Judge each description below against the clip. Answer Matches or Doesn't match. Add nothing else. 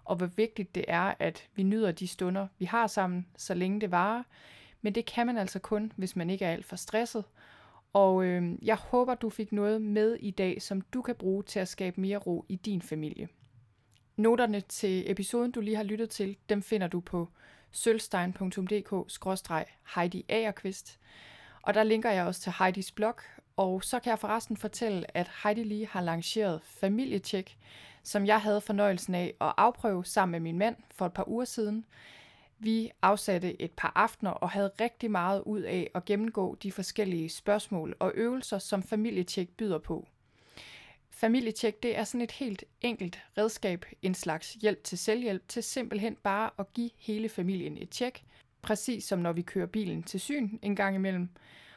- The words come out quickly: Doesn't match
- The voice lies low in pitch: Doesn't match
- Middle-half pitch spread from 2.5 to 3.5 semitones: Matches